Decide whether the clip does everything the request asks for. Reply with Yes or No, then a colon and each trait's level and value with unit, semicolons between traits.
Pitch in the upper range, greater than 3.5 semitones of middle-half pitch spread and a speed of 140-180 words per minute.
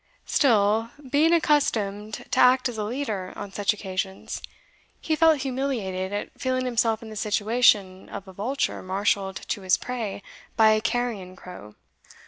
Yes: high, 215 Hz; average, 4.3 semitones; average, 150 wpm